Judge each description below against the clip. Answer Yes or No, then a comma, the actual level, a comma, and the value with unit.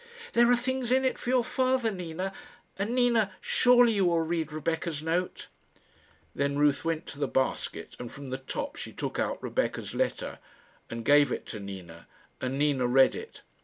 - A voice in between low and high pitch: Yes, medium, 165 Hz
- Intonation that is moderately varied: No, wide, 9.0 semitones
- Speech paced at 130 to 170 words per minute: No, average, 180 wpm